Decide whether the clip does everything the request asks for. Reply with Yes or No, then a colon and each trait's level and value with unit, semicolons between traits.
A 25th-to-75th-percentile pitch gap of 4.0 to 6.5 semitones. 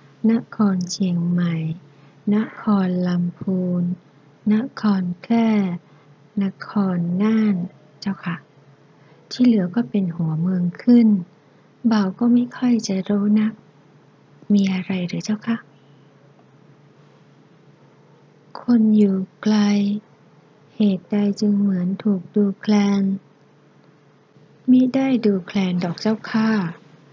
No: average, 3.6 semitones